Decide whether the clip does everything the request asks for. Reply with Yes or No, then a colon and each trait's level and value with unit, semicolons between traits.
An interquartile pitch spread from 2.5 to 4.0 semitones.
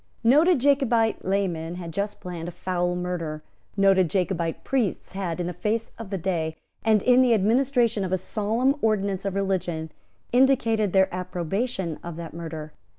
No: average, 4.4 semitones